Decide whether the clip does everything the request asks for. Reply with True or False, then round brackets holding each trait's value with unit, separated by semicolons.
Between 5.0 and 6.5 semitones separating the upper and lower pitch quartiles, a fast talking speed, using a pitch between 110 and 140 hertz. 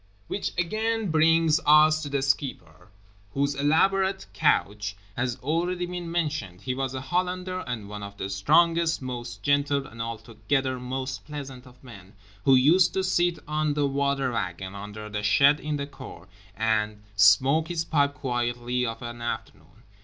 False (5.6 semitones; 155 wpm; 135 Hz)